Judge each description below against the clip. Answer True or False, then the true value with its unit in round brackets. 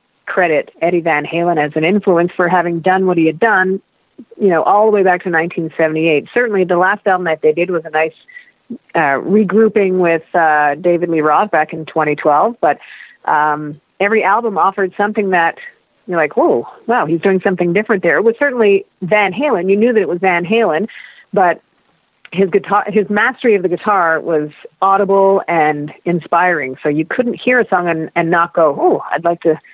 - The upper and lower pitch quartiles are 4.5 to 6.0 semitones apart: False (4.1 semitones)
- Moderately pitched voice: True (180 Hz)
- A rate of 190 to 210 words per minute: True (200 wpm)